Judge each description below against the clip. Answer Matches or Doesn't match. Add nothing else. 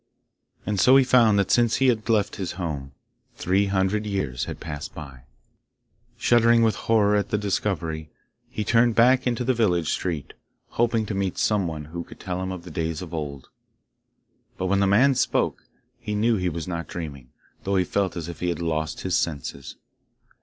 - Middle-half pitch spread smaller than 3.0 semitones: Doesn't match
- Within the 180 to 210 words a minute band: Matches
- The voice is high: Doesn't match